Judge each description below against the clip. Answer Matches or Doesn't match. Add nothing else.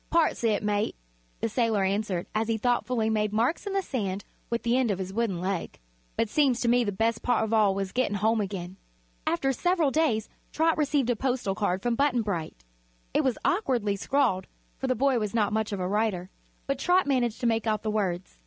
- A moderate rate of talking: Doesn't match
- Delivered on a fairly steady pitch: Doesn't match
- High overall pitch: Matches